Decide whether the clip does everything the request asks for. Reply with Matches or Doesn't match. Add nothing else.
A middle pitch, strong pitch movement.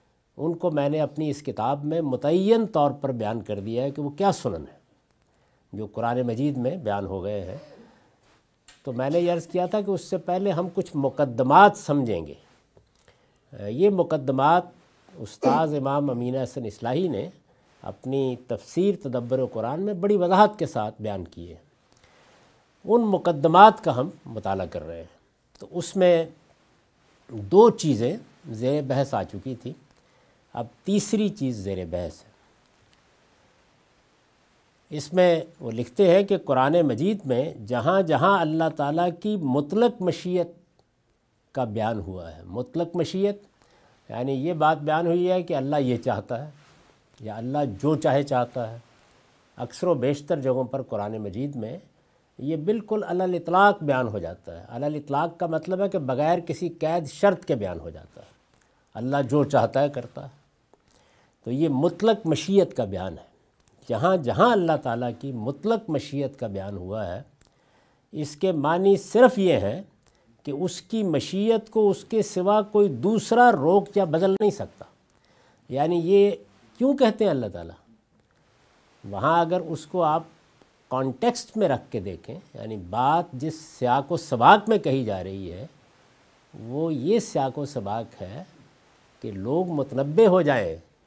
Matches